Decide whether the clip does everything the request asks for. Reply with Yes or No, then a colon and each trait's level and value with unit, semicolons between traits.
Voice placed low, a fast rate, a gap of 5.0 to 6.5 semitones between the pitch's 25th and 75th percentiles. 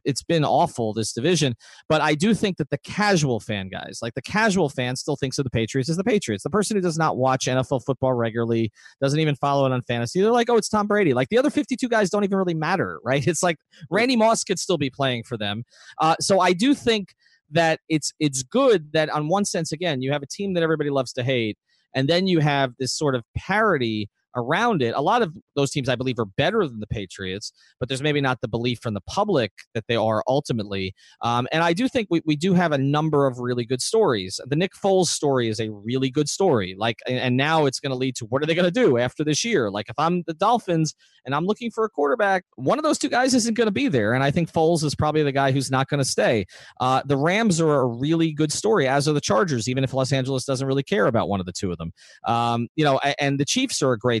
No: medium, 145 Hz; fast, 260 wpm; wide, 5.6 semitones